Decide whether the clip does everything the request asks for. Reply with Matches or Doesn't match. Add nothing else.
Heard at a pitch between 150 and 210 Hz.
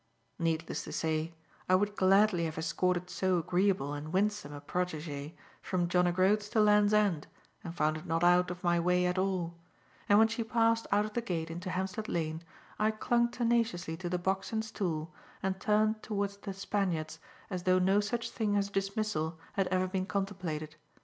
Matches